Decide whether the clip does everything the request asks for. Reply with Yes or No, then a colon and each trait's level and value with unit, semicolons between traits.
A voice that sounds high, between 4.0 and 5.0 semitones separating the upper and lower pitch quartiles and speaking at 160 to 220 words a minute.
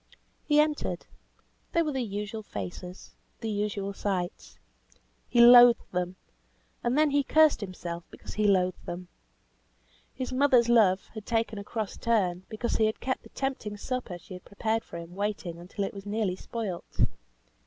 Yes: high, 210 Hz; average, 4.4 semitones; average, 165 wpm